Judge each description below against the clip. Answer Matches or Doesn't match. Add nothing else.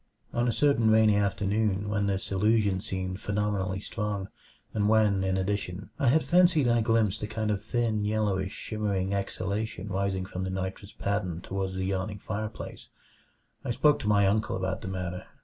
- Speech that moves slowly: Doesn't match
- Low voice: Matches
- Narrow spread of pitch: Matches